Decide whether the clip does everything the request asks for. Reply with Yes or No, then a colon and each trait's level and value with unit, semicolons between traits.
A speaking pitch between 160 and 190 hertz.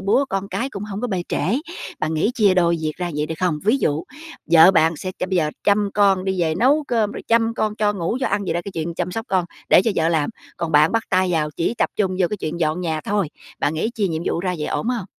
Yes: medium, 185 Hz